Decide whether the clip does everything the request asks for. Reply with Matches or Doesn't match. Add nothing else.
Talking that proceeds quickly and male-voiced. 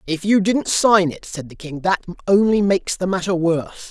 Matches